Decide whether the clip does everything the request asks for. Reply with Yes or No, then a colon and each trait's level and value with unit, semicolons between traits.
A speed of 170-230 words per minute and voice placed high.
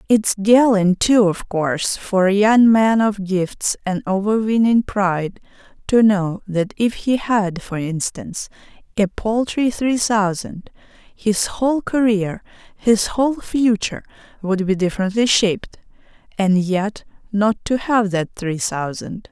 No: slow, 135 wpm; high, 205 Hz